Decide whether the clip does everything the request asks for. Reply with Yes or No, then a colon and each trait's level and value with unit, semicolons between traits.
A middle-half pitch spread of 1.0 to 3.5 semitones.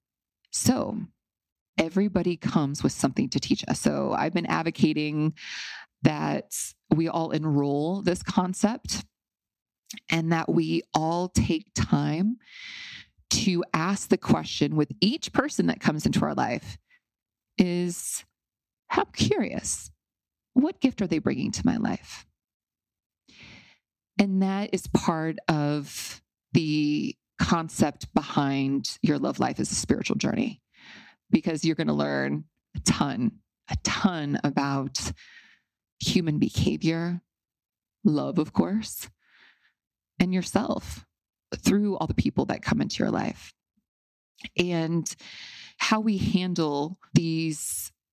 No: average, 4.7 semitones